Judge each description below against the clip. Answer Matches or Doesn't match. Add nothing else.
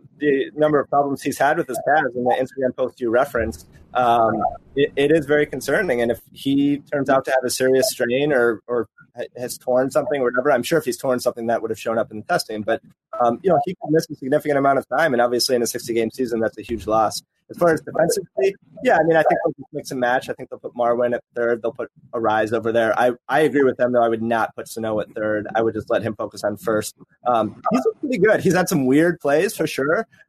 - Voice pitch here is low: Matches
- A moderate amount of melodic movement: Matches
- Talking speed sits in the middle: Doesn't match